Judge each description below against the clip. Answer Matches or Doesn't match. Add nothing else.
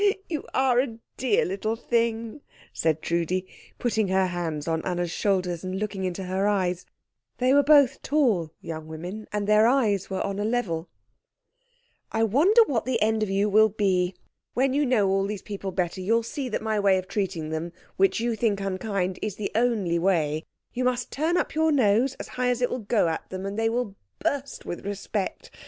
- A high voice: Matches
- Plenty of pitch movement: Doesn't match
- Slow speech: Doesn't match